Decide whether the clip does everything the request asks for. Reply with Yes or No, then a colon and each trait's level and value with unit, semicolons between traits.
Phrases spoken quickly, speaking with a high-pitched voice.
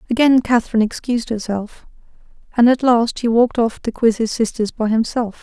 No: average, 175 wpm; high, 230 Hz